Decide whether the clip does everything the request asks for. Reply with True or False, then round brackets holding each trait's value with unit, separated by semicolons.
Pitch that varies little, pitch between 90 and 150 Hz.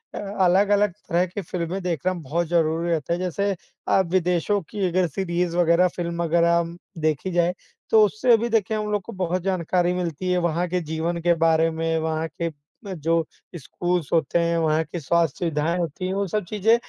False (2.0 semitones; 175 Hz)